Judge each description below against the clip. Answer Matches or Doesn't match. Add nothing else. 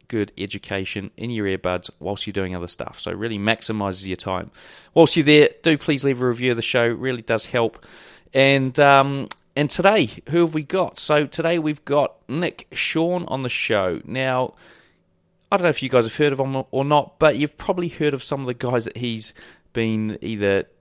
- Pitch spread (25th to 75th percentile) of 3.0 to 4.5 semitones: Doesn't match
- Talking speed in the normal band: Doesn't match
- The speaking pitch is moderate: Doesn't match